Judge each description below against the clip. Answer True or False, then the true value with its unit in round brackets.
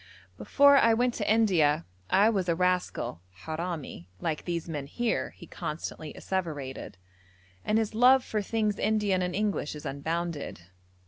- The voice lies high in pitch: False (180 Hz)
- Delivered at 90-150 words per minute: True (145 wpm)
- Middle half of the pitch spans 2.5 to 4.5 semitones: False (5.5 semitones)